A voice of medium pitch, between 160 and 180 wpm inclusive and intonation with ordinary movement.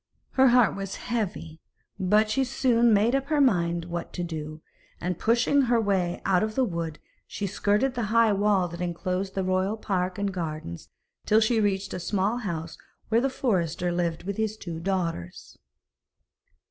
No: high, 195 Hz; average, 170 wpm; average, 4.4 semitones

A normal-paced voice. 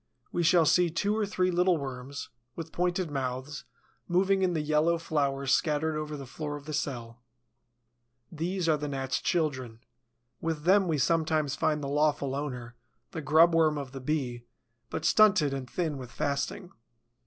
Yes: average, 165 wpm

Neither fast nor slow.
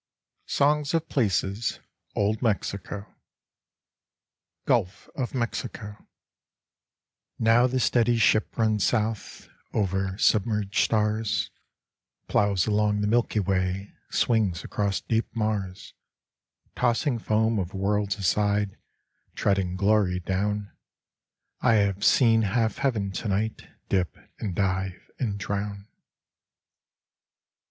No: slow, 100 wpm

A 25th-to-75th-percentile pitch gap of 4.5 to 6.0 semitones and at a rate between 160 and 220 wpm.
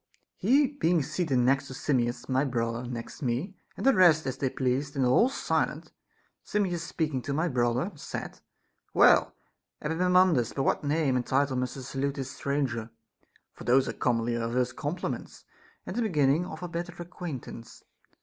Yes: average, 5.2 semitones; average, 170 wpm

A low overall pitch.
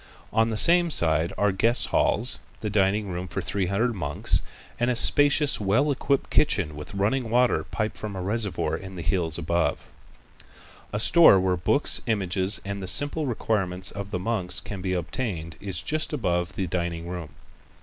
Yes: low, 100 Hz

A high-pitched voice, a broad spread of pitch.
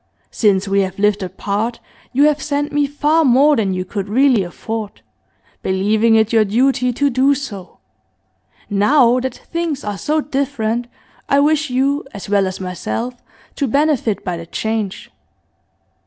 Yes: high, 235 Hz; wide, 5.7 semitones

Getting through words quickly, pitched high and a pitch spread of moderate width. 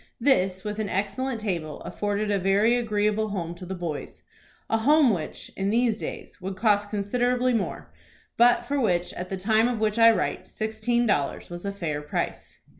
No: average, 185 wpm; high, 210 Hz; average, 3.6 semitones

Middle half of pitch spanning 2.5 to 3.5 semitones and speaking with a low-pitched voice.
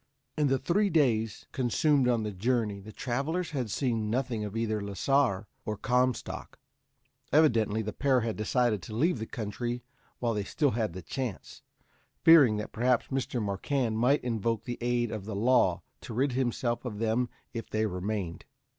Yes: average, 3.2 semitones; low, 120 Hz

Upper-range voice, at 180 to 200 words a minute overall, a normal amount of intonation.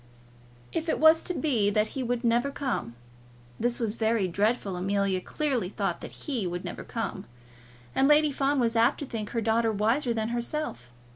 Yes: high, 235 Hz; average, 185 wpm; average, 4.7 semitones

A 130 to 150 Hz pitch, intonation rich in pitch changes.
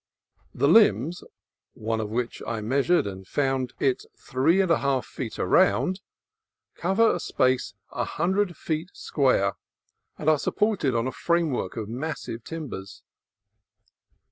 Yes: medium, 140 Hz; wide, 6.6 semitones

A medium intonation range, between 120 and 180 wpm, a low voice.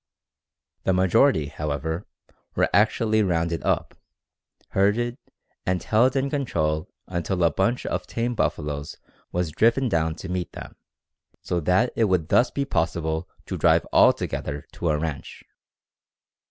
No: wide, 6.1 semitones; average, 140 wpm; very low, 90 Hz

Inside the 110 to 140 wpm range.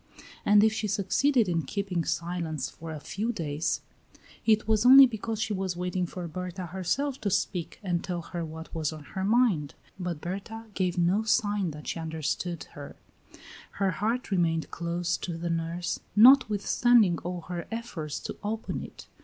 No: average, 170 wpm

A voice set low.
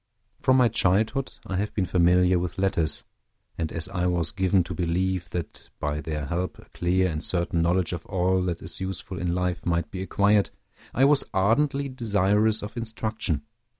Yes: very low, 95 Hz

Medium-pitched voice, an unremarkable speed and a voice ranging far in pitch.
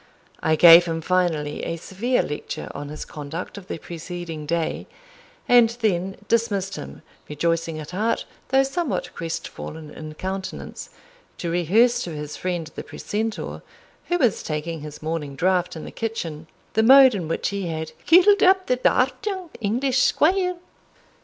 Yes: medium, 180 Hz; average, 155 wpm; wide, 6.9 semitones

